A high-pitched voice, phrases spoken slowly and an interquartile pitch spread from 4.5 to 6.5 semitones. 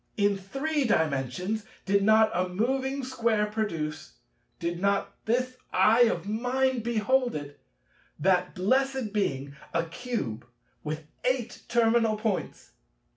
Yes: high, 215 Hz; slow, 110 wpm; wide, 5.6 semitones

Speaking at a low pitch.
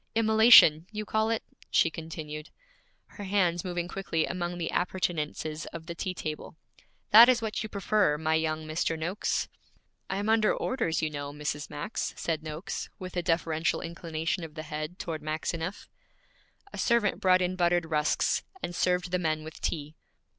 No: medium, 170 Hz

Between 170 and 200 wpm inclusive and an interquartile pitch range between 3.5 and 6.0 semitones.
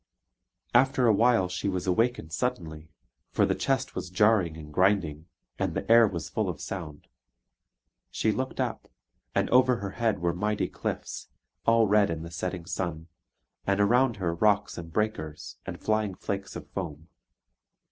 No: average, 160 wpm; average, 4.7 semitones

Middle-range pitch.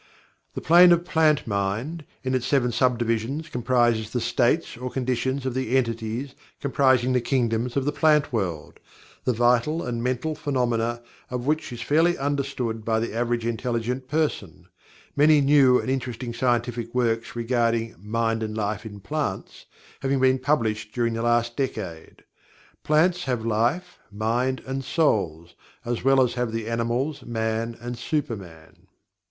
No: low, 120 Hz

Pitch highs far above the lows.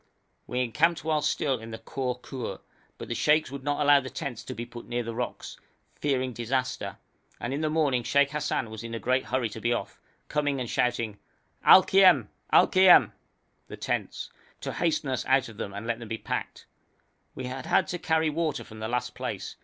No: average, 3.9 semitones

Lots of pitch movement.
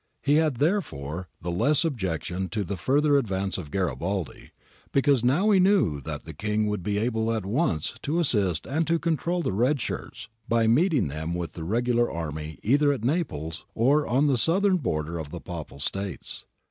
Yes: wide, 9.0 semitones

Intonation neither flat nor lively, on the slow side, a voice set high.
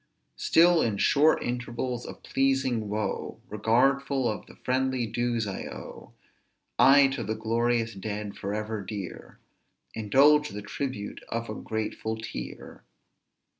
No: average, 3.6 semitones; slow, 130 wpm; low, 115 Hz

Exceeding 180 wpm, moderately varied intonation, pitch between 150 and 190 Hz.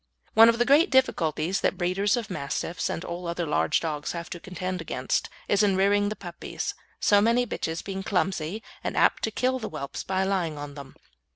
Yes: average, 200 wpm; average, 4.0 semitones; medium, 185 Hz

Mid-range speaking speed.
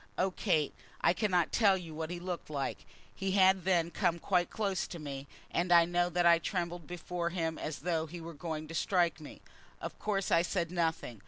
No: fast, 210 wpm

